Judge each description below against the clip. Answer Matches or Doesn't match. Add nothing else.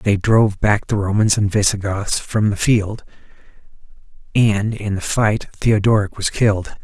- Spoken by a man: Matches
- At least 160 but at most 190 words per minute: Doesn't match